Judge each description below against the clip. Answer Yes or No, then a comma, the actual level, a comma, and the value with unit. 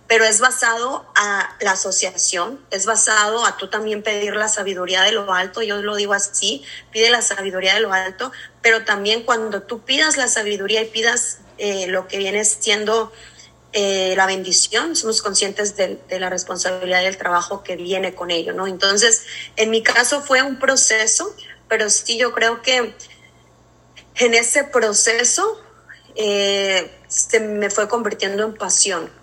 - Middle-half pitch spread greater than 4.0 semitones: No, average, 3.2 semitones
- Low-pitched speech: No, high, 210 Hz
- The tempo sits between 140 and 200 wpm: Yes, average, 165 wpm